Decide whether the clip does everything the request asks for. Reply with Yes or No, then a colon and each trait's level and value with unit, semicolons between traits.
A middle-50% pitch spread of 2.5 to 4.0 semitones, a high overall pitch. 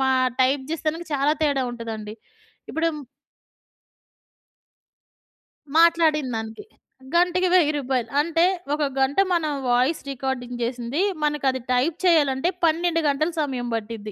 No: average, 4.6 semitones; very high, 280 Hz